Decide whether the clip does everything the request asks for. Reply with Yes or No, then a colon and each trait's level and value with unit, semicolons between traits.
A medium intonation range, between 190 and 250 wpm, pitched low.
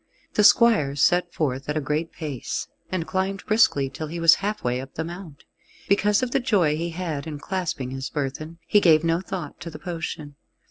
No: average, 4.4 semitones; average, 195 wpm; medium, 165 Hz